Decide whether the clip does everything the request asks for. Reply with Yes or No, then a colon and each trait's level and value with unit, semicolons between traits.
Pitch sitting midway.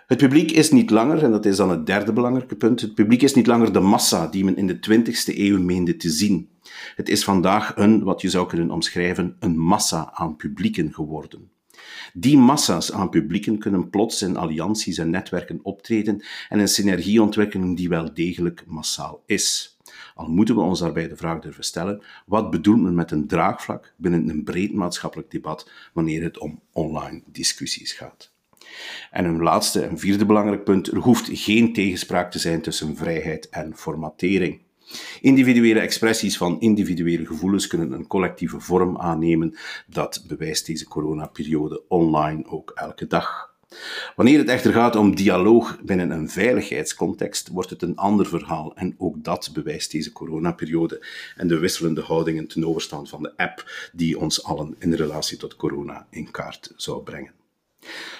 No: very low, 95 Hz